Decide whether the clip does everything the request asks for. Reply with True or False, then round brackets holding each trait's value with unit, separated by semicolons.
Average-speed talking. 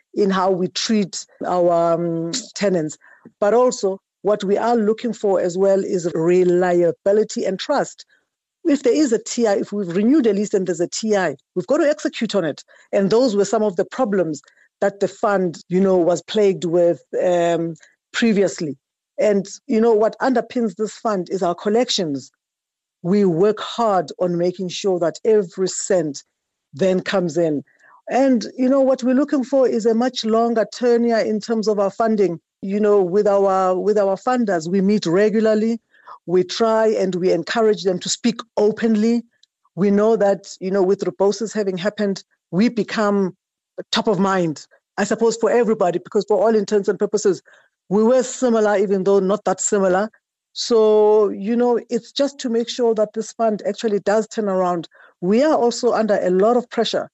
True (180 wpm)